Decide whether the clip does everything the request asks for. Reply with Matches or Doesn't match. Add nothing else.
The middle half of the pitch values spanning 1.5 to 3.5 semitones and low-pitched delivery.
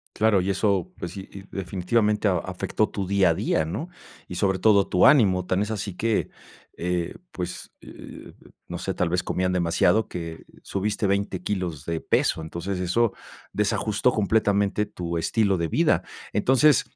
Matches